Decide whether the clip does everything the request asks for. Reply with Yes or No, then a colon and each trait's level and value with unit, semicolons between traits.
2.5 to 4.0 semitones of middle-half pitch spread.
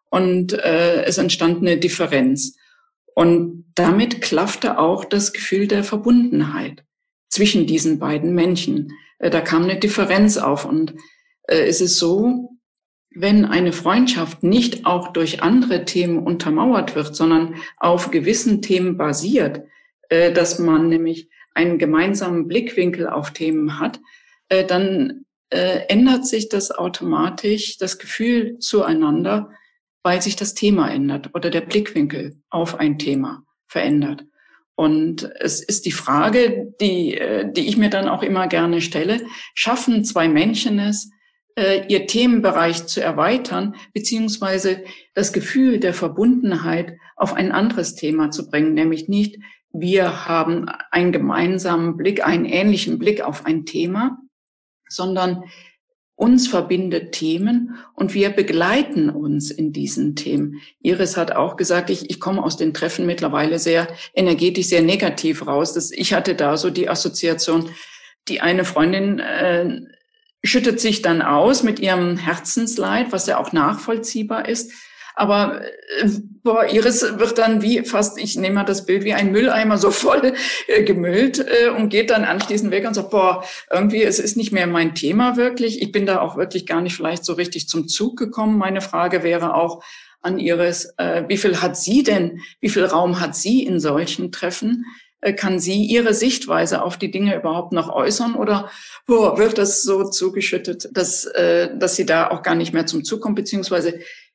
No: average, 4.8 semitones